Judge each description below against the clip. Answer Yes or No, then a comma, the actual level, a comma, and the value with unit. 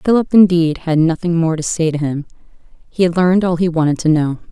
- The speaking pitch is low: No, medium, 170 Hz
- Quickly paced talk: Yes, fast, 225 wpm